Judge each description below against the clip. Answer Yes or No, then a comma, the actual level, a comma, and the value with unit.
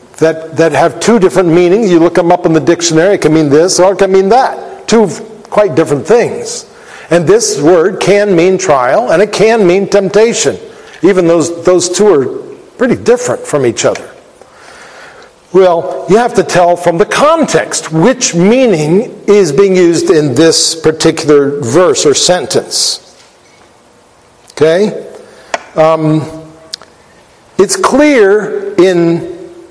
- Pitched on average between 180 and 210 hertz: Yes, high, 190 Hz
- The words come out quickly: No, average, 145 wpm